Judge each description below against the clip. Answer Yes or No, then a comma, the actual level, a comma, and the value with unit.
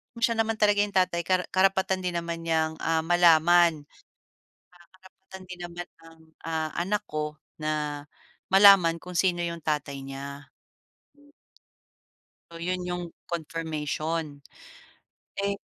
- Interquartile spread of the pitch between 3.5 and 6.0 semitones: No, average, 2.7 semitones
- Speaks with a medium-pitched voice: Yes, medium, 170 Hz